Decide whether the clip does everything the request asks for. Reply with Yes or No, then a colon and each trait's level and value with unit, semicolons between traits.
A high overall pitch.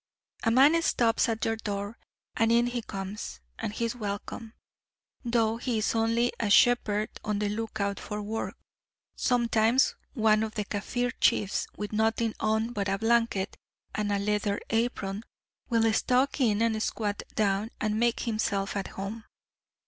Yes: high, 220 Hz